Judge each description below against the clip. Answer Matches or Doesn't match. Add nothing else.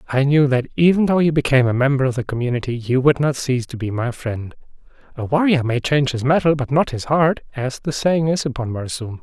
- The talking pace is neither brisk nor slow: Doesn't match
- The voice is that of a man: Matches